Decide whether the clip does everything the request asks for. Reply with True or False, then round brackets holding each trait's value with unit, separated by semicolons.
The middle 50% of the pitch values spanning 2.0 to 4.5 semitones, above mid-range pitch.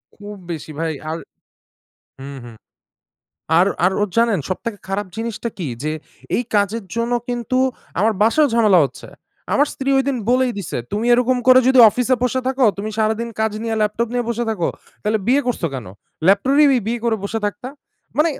True (3.6 semitones; 225 Hz)